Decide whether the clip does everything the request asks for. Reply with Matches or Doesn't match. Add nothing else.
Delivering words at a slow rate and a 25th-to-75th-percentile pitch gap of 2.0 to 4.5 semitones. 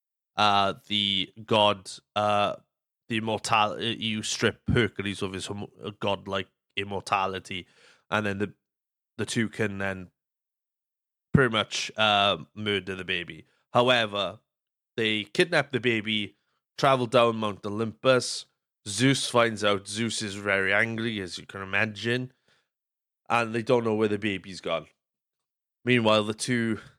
Matches